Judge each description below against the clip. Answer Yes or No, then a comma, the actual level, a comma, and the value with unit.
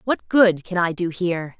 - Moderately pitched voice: Yes, medium, 180 Hz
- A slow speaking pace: No, fast, 225 wpm